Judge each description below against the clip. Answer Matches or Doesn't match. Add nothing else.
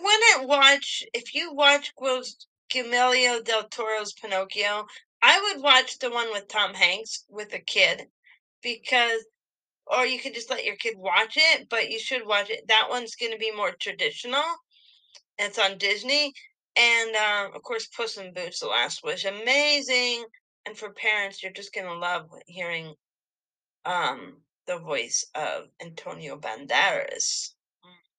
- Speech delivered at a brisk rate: Doesn't match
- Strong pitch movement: Matches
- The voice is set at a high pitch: Matches